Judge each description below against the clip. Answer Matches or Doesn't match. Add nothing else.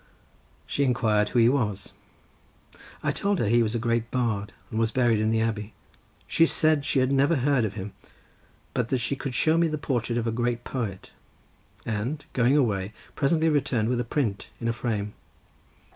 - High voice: Doesn't match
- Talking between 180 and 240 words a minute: Matches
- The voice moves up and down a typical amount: Matches